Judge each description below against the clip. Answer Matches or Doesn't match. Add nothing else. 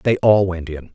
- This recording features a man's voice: Matches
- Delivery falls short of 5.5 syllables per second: Matches